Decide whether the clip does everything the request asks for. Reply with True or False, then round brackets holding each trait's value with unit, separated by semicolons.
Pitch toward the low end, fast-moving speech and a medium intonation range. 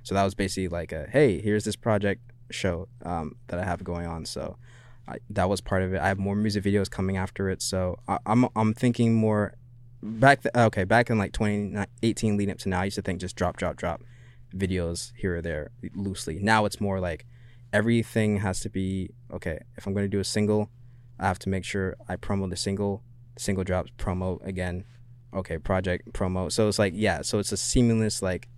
True (100 Hz; 215 wpm; 3.4 semitones)